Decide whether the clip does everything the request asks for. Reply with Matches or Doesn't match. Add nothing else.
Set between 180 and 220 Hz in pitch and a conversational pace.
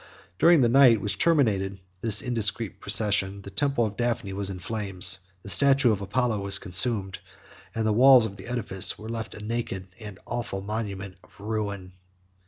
Doesn't match